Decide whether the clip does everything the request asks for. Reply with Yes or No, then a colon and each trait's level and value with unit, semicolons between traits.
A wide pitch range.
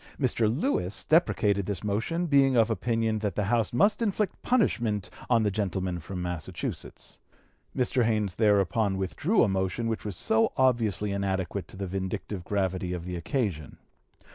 No: average, 3.9 semitones